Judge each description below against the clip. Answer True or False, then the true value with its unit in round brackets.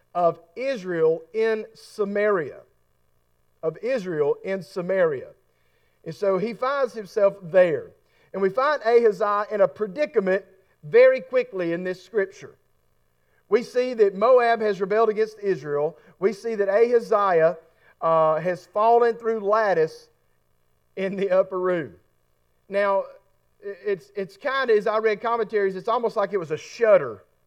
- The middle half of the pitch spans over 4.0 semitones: True (4.9 semitones)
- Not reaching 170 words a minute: True (140 wpm)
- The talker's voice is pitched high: True (200 Hz)